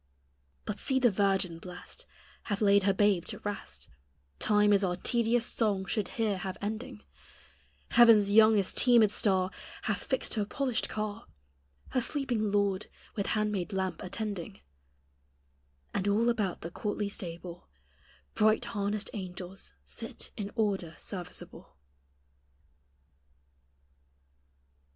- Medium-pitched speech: No, high, 205 Hz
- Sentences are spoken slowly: Yes, slow, 120 wpm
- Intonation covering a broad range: No, narrow, 2.4 semitones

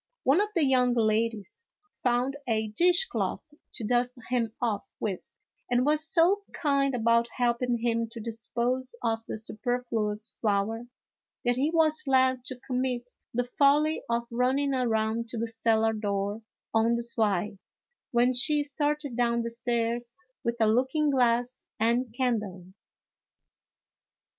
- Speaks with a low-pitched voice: No, high, 240 Hz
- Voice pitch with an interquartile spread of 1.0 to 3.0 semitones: Yes, narrow, 2.5 semitones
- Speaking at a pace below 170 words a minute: Yes, average, 140 wpm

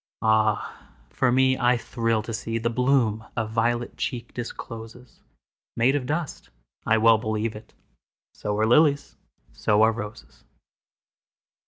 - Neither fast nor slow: No, slow, 115 wpm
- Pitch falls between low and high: No, low, 115 Hz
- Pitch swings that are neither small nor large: No, narrow, 2.2 semitones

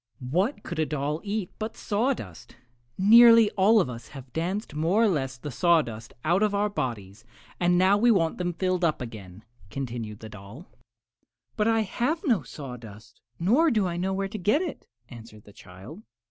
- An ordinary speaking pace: Yes, average, 175 wpm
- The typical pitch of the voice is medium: Yes, medium, 175 Hz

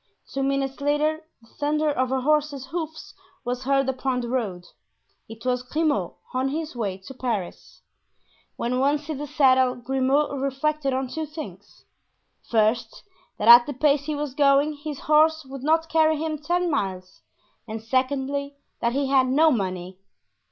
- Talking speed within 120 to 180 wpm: Yes, average, 160 wpm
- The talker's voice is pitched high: Yes, very high, 270 Hz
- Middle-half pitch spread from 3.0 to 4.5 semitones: Yes, average, 3.3 semitones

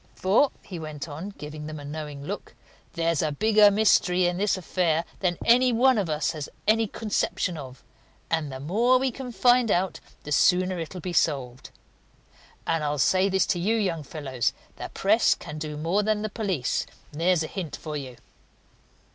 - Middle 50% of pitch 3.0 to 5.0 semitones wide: No, wide, 5.4 semitones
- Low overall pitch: No, medium, 175 Hz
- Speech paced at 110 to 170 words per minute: No, average, 180 wpm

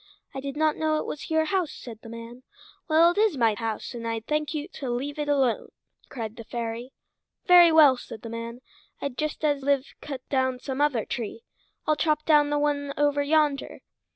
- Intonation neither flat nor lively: Yes, average, 4.1 semitones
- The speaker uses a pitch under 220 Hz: No, very high, 280 Hz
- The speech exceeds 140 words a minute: Yes, fast, 205 wpm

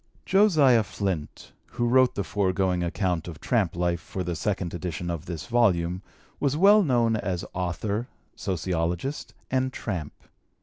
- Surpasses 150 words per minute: No, average, 140 wpm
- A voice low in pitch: Yes, very low, 95 Hz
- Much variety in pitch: Yes, wide, 5.7 semitones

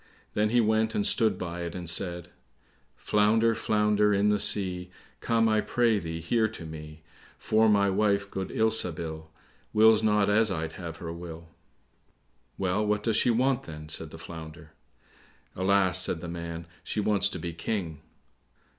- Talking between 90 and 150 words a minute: No, average, 165 wpm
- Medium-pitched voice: No, low, 100 Hz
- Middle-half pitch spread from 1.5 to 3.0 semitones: No, average, 4.3 semitones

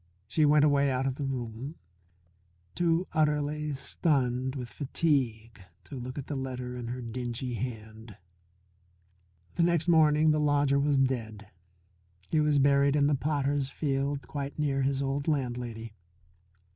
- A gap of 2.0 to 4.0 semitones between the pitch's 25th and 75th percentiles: Yes, average, 3.0 semitones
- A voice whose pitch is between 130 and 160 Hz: Yes, medium, 140 Hz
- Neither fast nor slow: Yes, average, 145 wpm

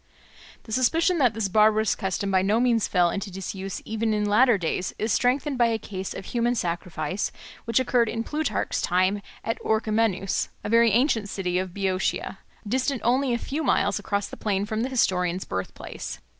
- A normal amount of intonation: Yes, average, 3.7 semitones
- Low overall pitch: No, high, 215 Hz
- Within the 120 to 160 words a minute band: No, average, 180 wpm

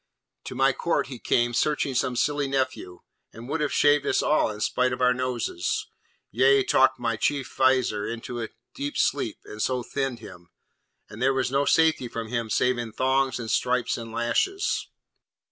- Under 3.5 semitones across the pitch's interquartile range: Yes, narrow, 2.5 semitones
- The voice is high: No, low, 125 Hz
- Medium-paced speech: Yes, average, 180 wpm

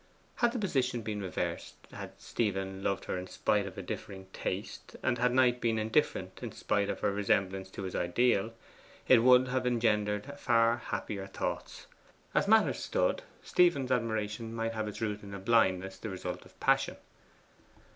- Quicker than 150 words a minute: Yes, average, 170 wpm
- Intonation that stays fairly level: No, average, 4.1 semitones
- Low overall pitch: Yes, low, 110 Hz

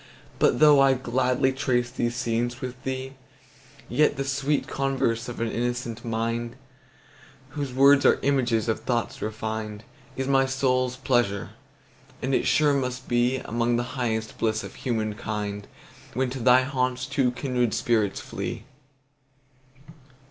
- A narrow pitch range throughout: Yes, narrow, 2.2 semitones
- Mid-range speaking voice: No, low, 125 Hz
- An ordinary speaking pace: No, slow, 125 wpm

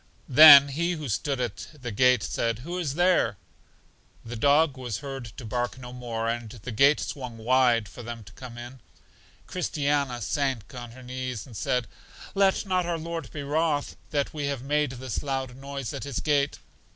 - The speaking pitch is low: Yes, low, 130 Hz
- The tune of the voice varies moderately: Yes, average, 3.3 semitones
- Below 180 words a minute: No, average, 185 wpm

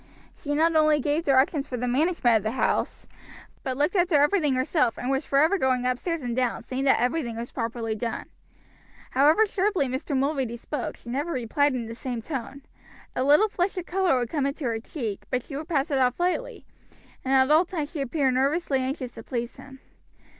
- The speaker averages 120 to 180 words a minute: No, fast, 205 wpm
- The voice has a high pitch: Yes, very high, 275 Hz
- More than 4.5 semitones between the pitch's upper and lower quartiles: No, average, 3.9 semitones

